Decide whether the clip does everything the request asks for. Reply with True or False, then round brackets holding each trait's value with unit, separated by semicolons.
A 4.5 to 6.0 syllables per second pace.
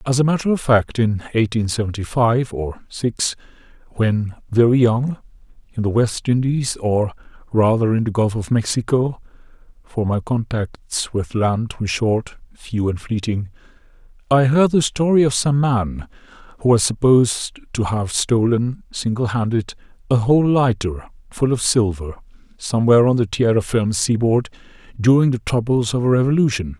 True (4.8 syllables/s)